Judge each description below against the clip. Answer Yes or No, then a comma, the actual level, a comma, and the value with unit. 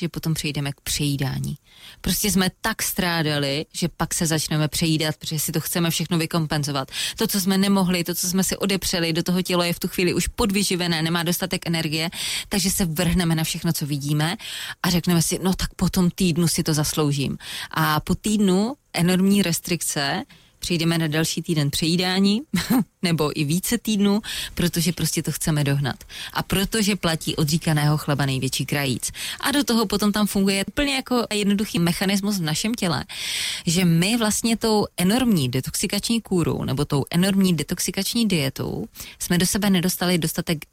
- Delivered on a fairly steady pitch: No, average, 3.6 semitones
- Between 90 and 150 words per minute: No, fast, 170 wpm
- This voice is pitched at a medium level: Yes, medium, 175 Hz